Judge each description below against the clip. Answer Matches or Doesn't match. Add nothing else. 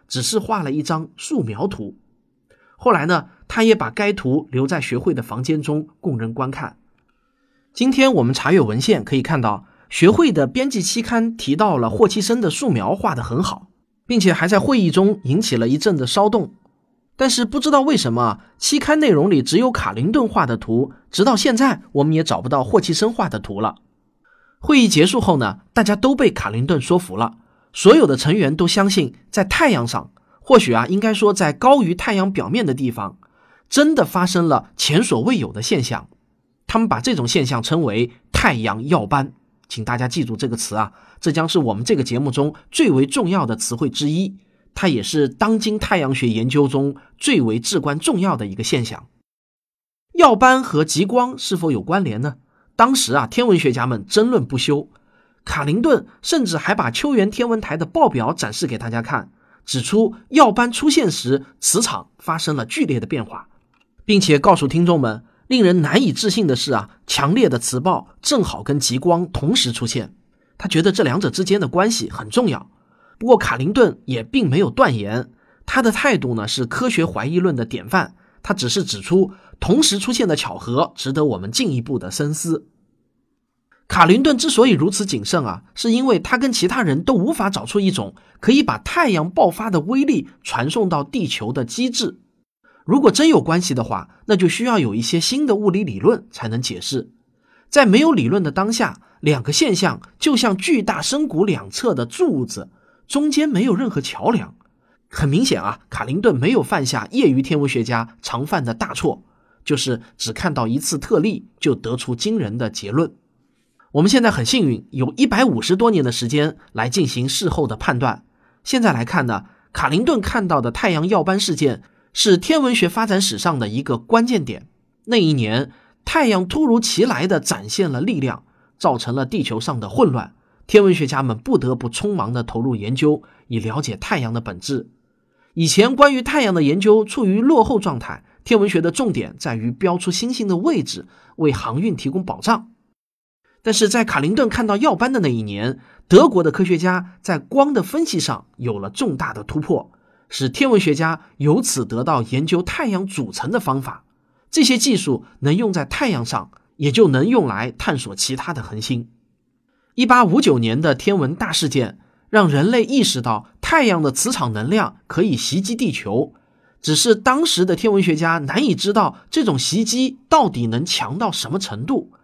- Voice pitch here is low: Doesn't match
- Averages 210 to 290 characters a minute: Matches